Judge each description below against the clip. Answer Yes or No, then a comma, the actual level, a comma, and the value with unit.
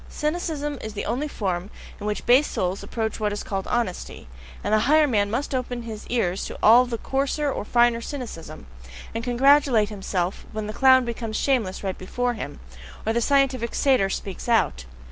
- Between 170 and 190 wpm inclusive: Yes, average, 185 wpm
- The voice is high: Yes, high, 230 Hz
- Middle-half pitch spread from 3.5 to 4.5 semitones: Yes, average, 4.1 semitones